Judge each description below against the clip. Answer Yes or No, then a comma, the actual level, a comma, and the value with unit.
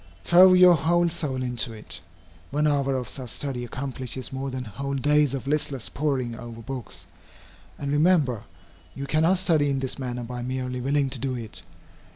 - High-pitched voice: No, low, 135 Hz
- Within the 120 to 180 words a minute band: Yes, average, 175 wpm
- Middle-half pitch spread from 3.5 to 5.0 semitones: No, average, 2.8 semitones